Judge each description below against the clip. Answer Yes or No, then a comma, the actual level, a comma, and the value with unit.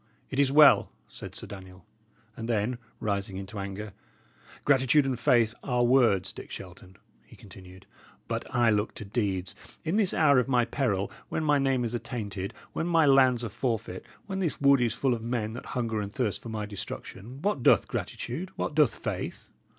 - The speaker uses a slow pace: No, average, 185 wpm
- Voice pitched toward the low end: Yes, low, 120 Hz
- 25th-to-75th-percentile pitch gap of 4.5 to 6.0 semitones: Yes, average, 4.9 semitones